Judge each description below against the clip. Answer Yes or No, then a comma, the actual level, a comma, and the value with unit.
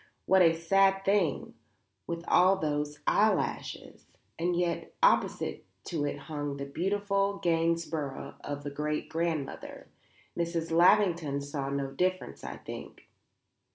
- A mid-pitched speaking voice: Yes, medium, 165 Hz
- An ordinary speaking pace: No, slow, 120 wpm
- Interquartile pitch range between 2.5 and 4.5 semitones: Yes, average, 3.9 semitones